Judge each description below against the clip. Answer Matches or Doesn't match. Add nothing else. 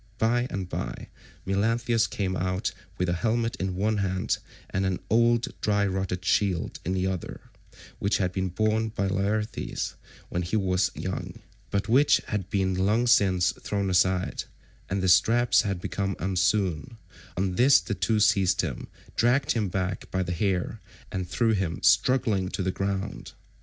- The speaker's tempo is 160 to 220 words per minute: Matches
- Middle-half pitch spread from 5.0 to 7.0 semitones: Doesn't match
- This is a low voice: Matches